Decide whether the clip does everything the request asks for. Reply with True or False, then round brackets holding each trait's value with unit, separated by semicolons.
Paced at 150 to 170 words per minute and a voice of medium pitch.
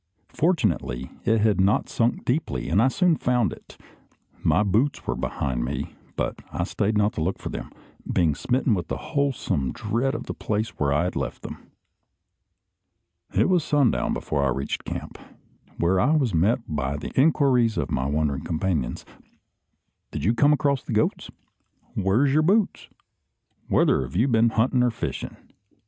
False (165 wpm; 110 Hz)